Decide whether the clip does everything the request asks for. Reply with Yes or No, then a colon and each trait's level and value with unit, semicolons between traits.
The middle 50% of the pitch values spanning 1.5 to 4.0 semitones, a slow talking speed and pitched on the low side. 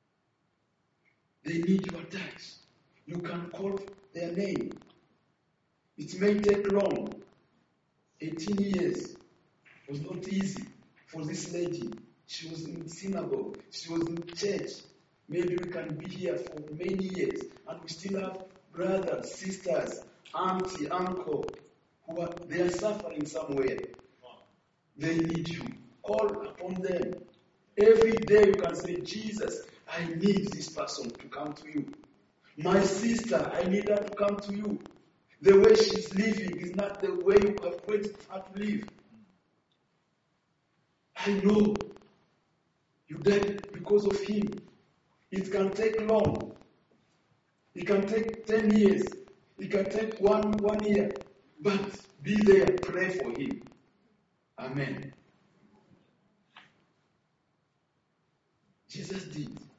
No: average, 3.0 semitones; slow, 125 wpm; high, 190 Hz